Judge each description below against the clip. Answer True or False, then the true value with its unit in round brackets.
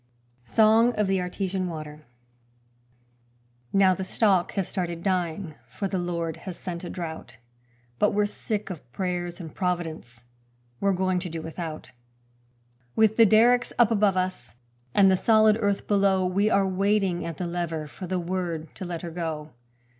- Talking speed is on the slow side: False (160 wpm)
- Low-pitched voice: False (185 Hz)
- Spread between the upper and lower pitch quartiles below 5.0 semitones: True (2.8 semitones)